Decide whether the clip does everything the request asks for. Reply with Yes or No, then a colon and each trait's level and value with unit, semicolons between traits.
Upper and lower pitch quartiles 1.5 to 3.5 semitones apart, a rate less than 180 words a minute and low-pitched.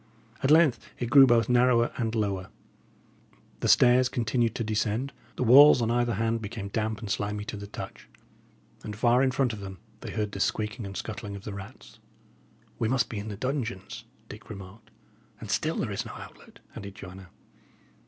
No: average, 3.0 semitones; average, 185 wpm; low, 110 Hz